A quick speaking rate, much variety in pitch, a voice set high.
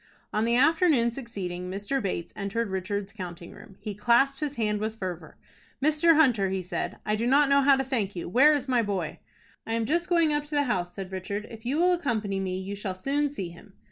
Yes: fast, 225 wpm; wide, 6.3 semitones; high, 225 Hz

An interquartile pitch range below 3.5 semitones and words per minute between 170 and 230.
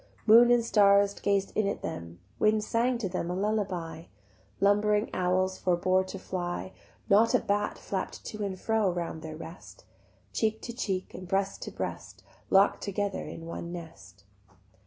No: average, 2.8 semitones; average, 155 wpm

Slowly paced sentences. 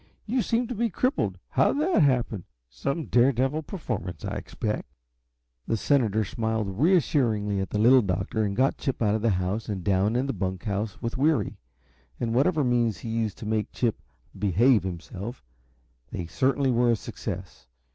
No: average, 175 wpm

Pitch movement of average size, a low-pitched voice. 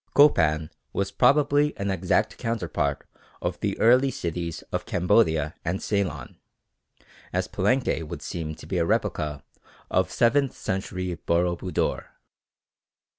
No: wide, 5.9 semitones; very low, 90 Hz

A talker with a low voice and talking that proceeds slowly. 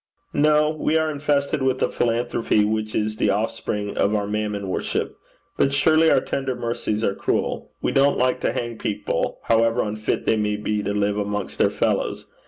No: low, 115 Hz; average, 185 wpm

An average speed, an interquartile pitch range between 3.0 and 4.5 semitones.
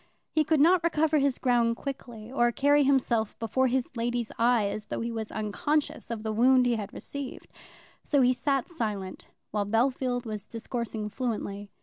Yes: average, 175 wpm; average, 3.6 semitones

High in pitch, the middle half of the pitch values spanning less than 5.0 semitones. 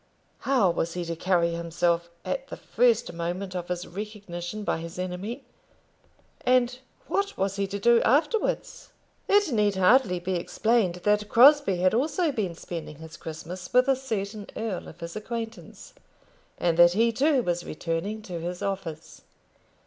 No: high, 195 Hz; average, 5.3 semitones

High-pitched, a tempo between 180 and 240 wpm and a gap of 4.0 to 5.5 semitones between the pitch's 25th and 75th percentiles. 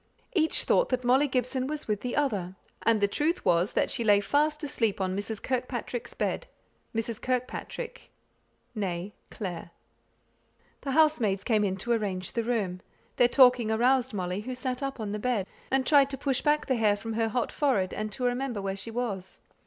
Yes: high, 235 Hz; average, 185 wpm; average, 4.4 semitones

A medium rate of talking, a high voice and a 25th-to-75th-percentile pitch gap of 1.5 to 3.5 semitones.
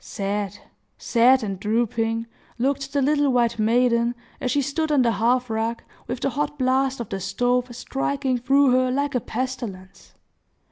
Yes: average, 160 wpm; very high, 250 Hz; average, 2.9 semitones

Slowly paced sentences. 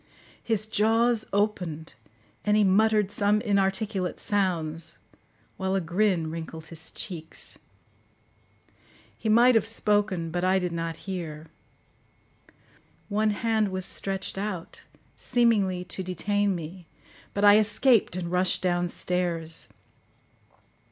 Yes: slow, 110 wpm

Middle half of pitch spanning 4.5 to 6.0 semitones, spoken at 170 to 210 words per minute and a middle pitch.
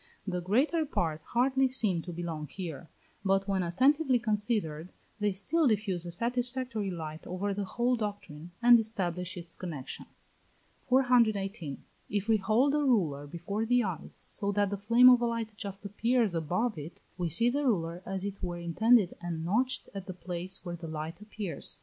No: average, 5.3 semitones; average, 175 wpm; high, 200 Hz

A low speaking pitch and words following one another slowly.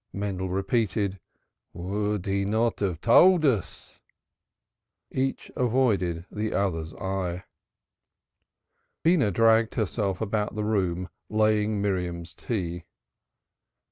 Yes: low, 100 Hz; slow, 95 wpm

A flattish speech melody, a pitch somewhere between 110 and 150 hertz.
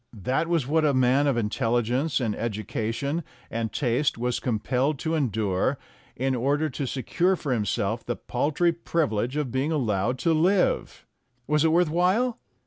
No: average, 5.1 semitones; low, 135 Hz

